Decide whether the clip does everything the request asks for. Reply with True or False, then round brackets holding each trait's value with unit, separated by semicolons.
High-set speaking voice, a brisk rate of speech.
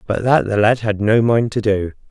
False (110 Hz; 255 wpm)